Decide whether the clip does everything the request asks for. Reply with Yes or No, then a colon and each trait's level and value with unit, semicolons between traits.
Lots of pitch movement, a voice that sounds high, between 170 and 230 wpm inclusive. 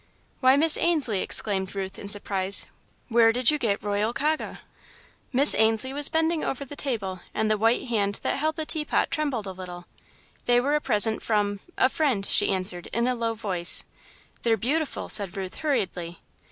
Yes: wide, 5.9 semitones; high, 225 Hz; average, 180 wpm